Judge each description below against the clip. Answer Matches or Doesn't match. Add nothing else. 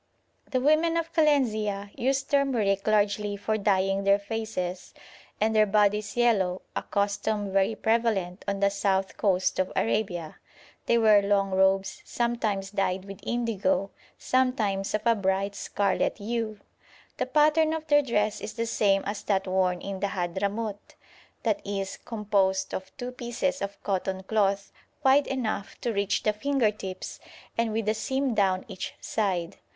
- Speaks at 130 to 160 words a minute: Matches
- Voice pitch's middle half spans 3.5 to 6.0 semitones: Doesn't match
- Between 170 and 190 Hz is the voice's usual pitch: Doesn't match